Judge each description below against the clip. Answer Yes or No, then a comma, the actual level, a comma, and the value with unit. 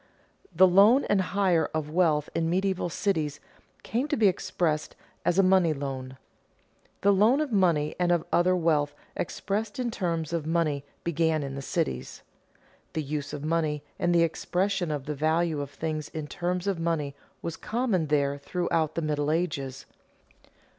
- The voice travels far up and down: No, average, 3.7 semitones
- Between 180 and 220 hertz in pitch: No, medium, 165 Hz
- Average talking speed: Yes, average, 165 wpm